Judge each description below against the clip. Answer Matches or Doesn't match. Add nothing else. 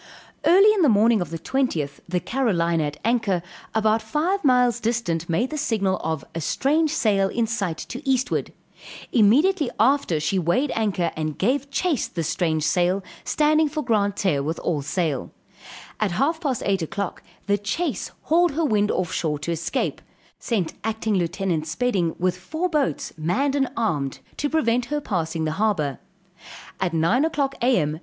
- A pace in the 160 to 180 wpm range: Matches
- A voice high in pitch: Matches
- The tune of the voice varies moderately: Doesn't match